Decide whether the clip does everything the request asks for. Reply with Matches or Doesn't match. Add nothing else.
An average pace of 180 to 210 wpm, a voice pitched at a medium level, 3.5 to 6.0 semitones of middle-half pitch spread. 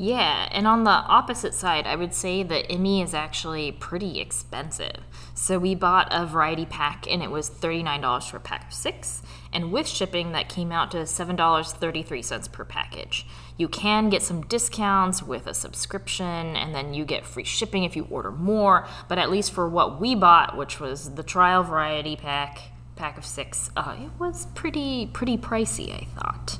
Matches